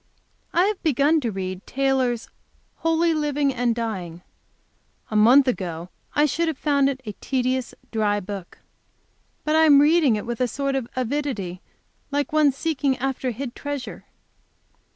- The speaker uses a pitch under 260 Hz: No, very high, 265 Hz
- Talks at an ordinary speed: Yes, average, 150 wpm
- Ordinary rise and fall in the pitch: Yes, average, 4.6 semitones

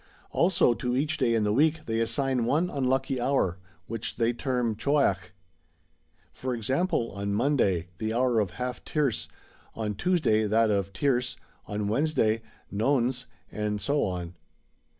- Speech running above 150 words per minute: No, average, 145 wpm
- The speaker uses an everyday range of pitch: Yes, average, 4.4 semitones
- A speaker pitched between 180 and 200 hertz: No, low, 120 Hz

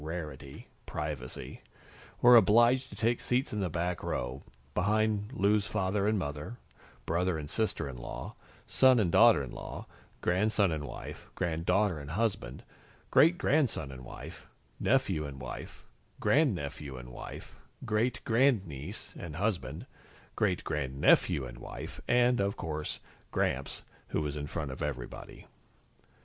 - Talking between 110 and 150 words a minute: Yes, slow, 135 wpm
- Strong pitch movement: Yes, wide, 7.1 semitones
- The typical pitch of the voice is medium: No, very low, 90 Hz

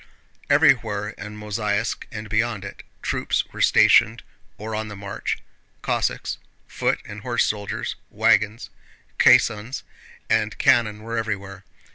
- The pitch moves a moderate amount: No, narrow, 1.8 semitones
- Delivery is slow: Yes, slow, 120 wpm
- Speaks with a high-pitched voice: No, low, 105 Hz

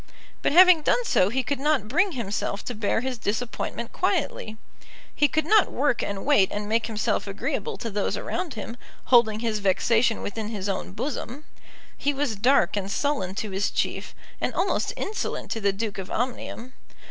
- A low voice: No, high, 230 Hz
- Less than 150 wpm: No, average, 180 wpm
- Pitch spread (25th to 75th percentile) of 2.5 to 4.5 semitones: No, wide, 5.4 semitones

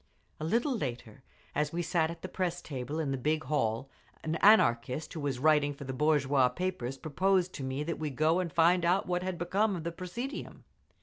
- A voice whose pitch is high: No, medium, 155 Hz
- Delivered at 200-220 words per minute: Yes, fast, 205 wpm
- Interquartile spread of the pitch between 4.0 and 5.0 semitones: Yes, average, 4.6 semitones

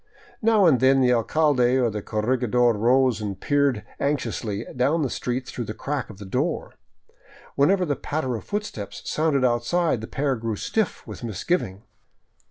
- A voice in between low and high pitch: No, low, 125 Hz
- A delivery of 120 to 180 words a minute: Yes, average, 170 wpm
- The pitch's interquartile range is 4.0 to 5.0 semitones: Yes, average, 4.5 semitones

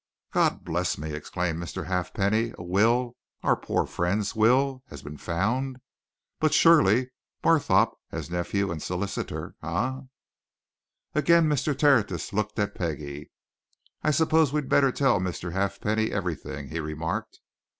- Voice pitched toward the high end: No, low, 100 Hz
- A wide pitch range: Yes, wide, 6.9 semitones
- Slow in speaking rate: Yes, slow, 130 wpm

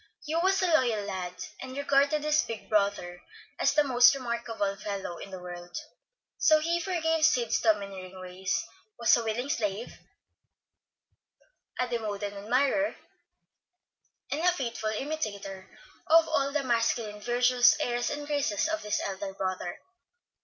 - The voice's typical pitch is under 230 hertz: No, high, 235 Hz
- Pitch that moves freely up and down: Yes, wide, 6.4 semitones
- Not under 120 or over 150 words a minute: Yes, average, 140 wpm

